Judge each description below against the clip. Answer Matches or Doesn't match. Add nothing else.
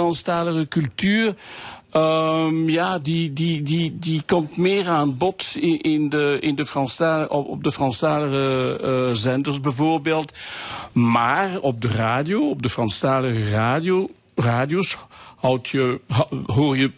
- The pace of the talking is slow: Matches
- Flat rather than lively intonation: Doesn't match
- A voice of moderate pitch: Matches